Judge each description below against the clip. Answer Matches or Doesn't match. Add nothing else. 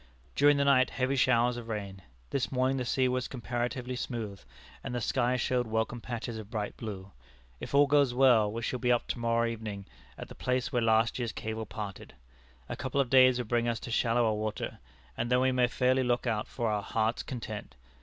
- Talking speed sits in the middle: Doesn't match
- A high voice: Doesn't match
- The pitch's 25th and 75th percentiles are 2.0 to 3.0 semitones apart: Matches